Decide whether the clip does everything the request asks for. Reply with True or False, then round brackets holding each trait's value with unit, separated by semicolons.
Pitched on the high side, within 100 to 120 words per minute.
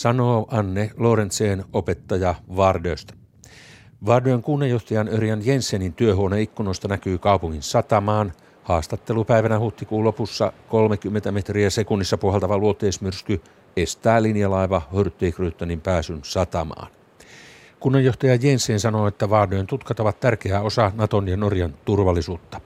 False (105 Hz; 105 wpm)